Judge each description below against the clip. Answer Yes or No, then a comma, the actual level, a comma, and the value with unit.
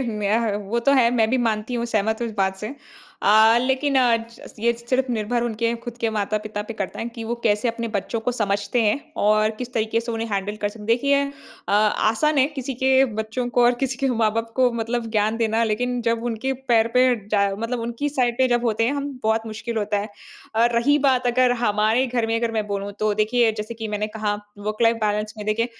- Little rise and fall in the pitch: Yes, narrow, 2.3 semitones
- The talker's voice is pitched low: No, high, 230 Hz